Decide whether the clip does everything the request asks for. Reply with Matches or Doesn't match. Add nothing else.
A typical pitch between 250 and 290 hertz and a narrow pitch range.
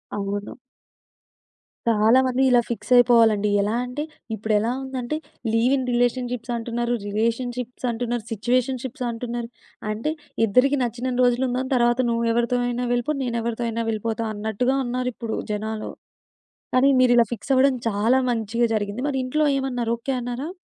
Doesn't match